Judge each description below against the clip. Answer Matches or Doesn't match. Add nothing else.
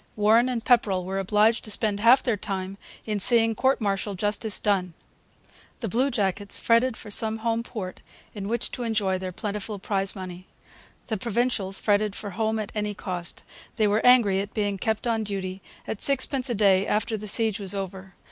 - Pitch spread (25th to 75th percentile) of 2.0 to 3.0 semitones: Matches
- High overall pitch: Matches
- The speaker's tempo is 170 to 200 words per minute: Matches